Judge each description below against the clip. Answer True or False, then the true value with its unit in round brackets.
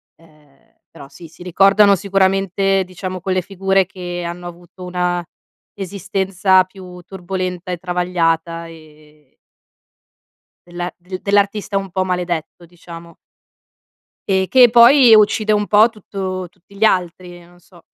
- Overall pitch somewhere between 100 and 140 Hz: False (185 Hz)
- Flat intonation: True (1.9 semitones)